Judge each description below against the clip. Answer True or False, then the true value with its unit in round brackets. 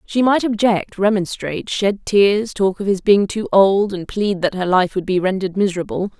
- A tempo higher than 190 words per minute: True (205 wpm)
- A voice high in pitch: True (195 Hz)